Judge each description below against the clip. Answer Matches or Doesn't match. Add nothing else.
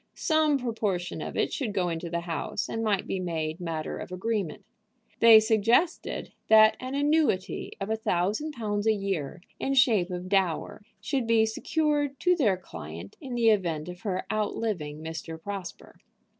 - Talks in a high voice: Matches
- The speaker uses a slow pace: Doesn't match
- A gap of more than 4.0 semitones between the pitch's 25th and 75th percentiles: Matches